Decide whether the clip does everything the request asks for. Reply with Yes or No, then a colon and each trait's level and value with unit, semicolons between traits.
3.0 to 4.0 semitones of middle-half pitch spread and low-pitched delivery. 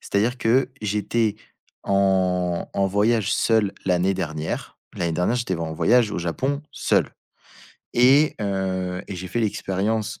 Yes: average, 3.7 semitones; low, 100 Hz